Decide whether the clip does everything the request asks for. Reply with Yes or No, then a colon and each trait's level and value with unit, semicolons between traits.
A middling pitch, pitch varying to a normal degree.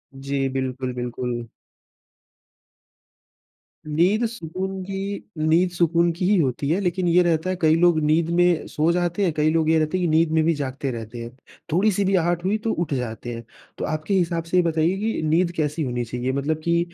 Yes: medium, 160 Hz; average, 4.1 semitones